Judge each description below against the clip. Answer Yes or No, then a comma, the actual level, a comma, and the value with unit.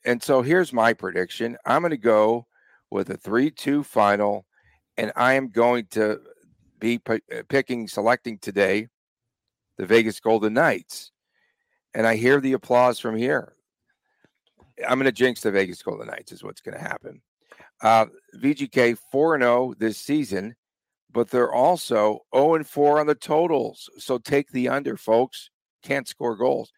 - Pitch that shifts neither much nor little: Yes, average, 3.1 semitones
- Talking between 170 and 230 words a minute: No, average, 155 wpm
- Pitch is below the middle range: Yes, low, 120 Hz